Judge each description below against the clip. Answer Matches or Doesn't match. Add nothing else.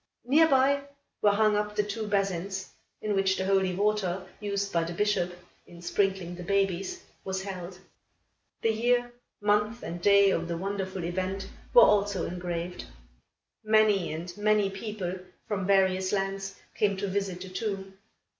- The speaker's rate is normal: Matches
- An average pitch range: Doesn't match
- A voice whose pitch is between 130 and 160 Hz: Doesn't match